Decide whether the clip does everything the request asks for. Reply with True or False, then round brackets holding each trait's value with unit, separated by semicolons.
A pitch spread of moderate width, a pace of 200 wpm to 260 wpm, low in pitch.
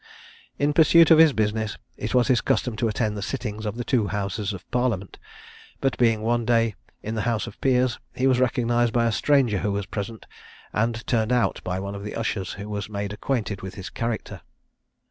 True (3.0 semitones; 205 wpm; 110 Hz)